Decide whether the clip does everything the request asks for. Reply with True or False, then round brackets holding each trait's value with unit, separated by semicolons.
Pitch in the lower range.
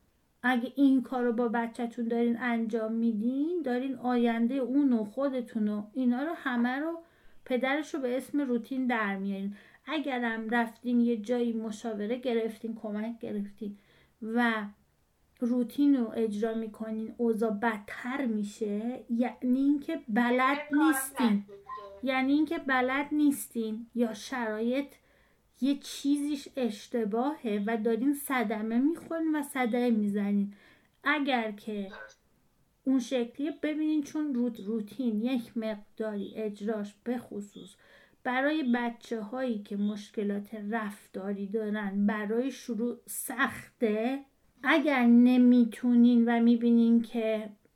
False (240 Hz)